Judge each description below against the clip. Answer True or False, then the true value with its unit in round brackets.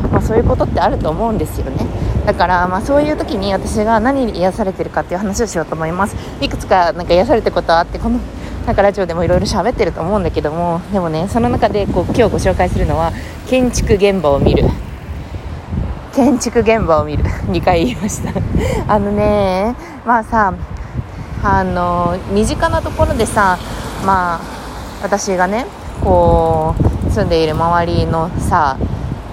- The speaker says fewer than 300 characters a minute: False (345 characters per minute)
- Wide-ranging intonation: False (4.7 semitones)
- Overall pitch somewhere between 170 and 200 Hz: True (185 Hz)